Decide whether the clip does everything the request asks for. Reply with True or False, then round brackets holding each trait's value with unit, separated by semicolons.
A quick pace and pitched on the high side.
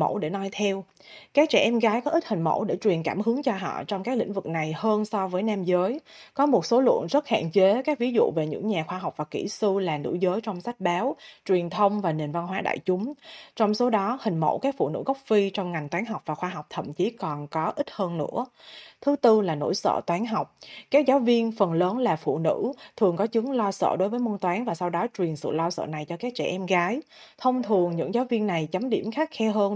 True (265 wpm; 205 Hz)